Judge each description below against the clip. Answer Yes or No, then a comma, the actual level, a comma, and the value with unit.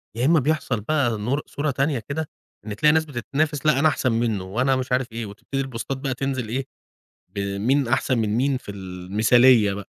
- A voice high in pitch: No, low, 130 Hz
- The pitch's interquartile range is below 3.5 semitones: No, average, 4.2 semitones